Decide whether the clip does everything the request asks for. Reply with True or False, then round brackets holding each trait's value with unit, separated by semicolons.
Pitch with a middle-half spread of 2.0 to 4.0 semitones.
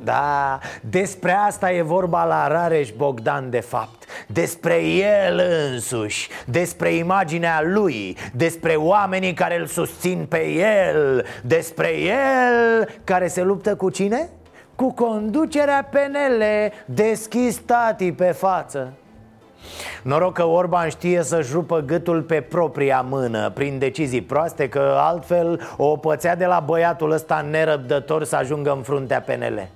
False (5.1 semitones)